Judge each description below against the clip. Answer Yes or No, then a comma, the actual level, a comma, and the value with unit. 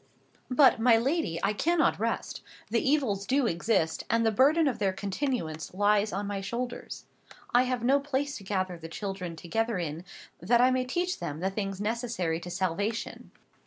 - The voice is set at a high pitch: Yes, high, 215 Hz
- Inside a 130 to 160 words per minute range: No, average, 175 wpm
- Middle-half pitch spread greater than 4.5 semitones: Yes, average, 5.2 semitones